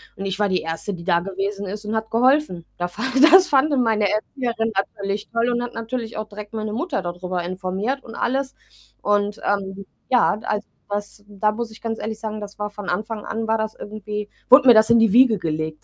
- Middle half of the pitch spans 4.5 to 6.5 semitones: No, average, 2.7 semitones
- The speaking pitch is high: Yes, high, 215 Hz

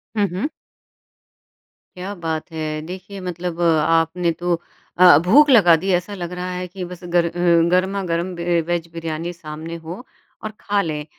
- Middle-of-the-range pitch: Yes, medium, 175 Hz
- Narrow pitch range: Yes, narrow, 1.7 semitones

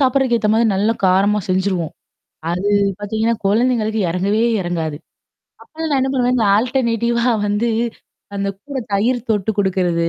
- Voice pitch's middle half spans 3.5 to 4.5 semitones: Yes, average, 3.9 semitones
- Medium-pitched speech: No, high, 215 Hz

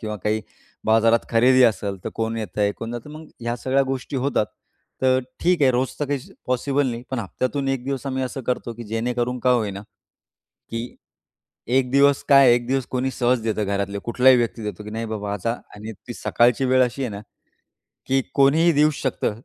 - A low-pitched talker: Yes, low, 125 Hz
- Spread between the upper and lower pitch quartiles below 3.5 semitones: Yes, average, 2.9 semitones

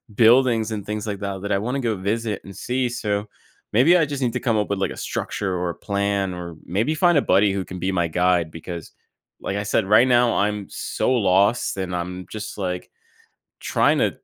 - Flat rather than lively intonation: No, average, 3.7 semitones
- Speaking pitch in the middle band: No, low, 100 Hz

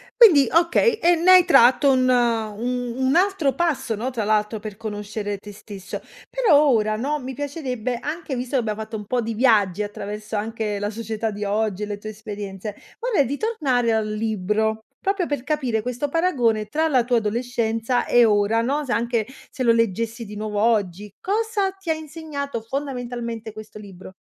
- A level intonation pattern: No, average, 4.9 semitones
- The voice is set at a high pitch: Yes, high, 235 Hz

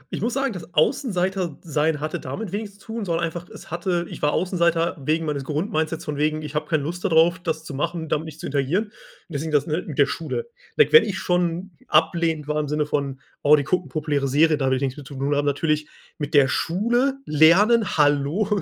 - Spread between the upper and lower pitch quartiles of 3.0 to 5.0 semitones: Yes, average, 3.4 semitones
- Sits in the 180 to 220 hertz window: No, medium, 160 Hz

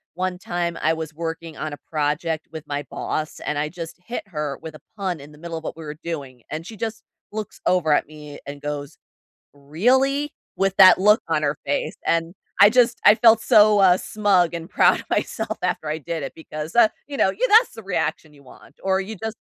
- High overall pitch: No, medium, 165 Hz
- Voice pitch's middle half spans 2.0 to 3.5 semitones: No, average, 5.1 semitones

